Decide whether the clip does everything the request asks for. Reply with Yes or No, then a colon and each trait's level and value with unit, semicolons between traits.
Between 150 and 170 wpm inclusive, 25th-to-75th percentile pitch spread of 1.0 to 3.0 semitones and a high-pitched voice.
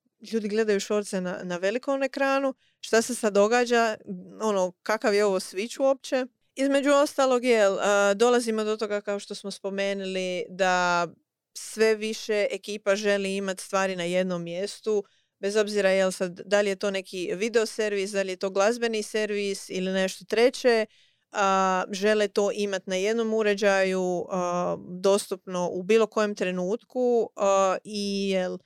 Yes: average, 155 wpm; narrow, 2.6 semitones; high, 205 Hz